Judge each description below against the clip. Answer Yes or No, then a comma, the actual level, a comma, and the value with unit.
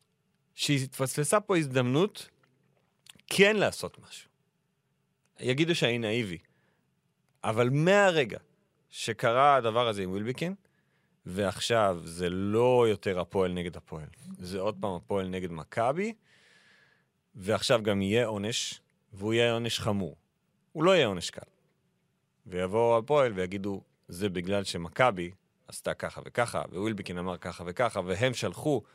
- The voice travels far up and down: Yes, wide, 6.0 semitones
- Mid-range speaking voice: No, low, 110 Hz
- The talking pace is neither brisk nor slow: Yes, average, 120 wpm